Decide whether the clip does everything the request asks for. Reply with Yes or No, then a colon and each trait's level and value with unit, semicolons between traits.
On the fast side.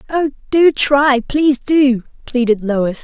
No: average, 140 wpm